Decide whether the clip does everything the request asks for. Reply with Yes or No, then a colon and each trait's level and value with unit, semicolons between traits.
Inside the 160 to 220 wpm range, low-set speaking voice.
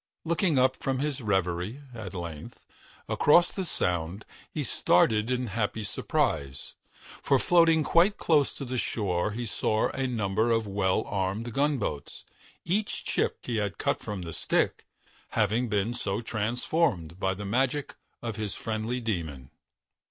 No: average, 150 wpm; low, 110 Hz